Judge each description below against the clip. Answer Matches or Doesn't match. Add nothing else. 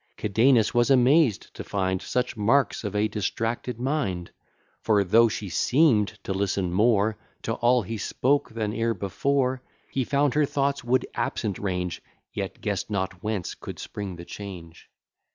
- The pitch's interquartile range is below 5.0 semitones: Matches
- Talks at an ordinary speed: Matches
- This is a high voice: Doesn't match